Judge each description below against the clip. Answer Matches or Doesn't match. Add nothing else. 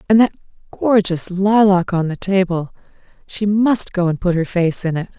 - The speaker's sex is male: Doesn't match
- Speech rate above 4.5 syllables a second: Matches